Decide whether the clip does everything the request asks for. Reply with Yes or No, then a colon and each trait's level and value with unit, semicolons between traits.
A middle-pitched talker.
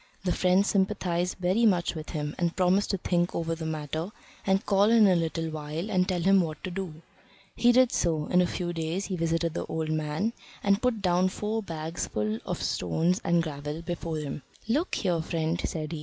Yes: medium, 175 Hz